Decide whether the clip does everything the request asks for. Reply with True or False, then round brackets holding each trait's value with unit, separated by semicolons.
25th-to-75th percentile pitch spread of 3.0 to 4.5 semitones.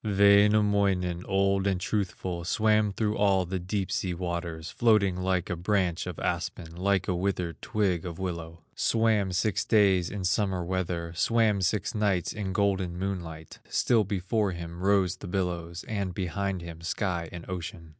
False (2.5 semitones)